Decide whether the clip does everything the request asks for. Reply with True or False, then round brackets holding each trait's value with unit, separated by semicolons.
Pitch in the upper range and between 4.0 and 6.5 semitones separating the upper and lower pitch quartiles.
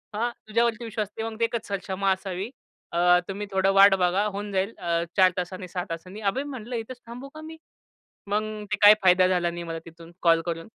False (195 Hz; 3.6 semitones)